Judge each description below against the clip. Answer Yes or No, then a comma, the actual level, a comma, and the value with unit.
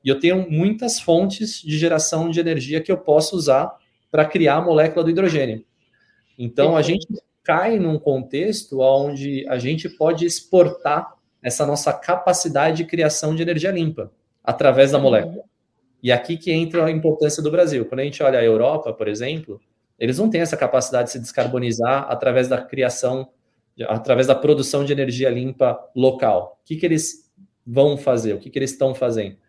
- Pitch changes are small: No, average, 4.3 semitones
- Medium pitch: Yes, medium, 145 Hz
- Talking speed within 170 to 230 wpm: Yes, average, 180 wpm